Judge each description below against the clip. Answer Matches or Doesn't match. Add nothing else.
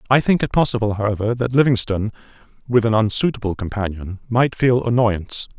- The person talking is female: Doesn't match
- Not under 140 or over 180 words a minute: Matches